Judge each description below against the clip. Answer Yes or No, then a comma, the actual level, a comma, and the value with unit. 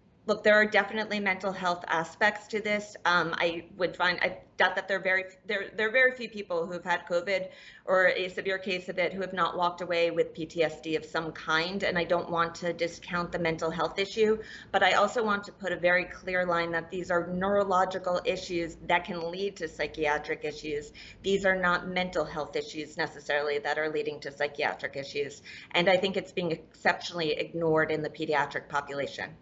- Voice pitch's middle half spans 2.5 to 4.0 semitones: Yes, average, 2.8 semitones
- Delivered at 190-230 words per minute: Yes, average, 200 wpm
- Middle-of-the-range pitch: Yes, medium, 175 Hz